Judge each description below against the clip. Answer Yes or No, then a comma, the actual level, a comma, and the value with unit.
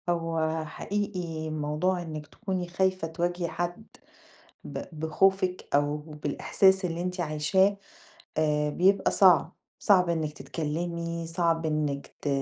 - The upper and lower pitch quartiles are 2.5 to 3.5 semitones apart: Yes, average, 2.9 semitones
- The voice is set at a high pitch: No, medium, 170 Hz